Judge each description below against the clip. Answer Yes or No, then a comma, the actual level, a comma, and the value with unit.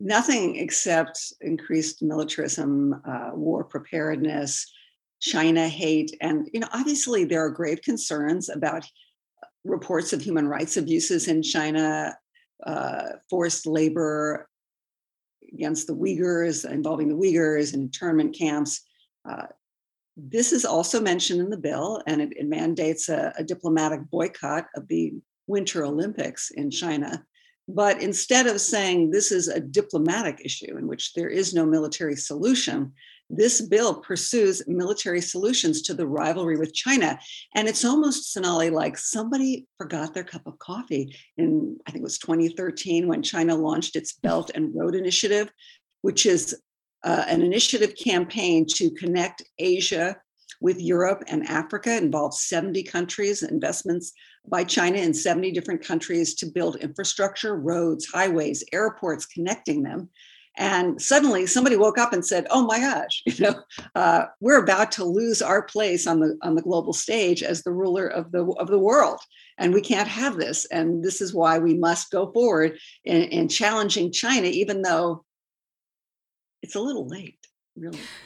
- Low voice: No, medium, 185 Hz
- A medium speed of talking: Yes, average, 150 wpm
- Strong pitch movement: Yes, wide, 8.2 semitones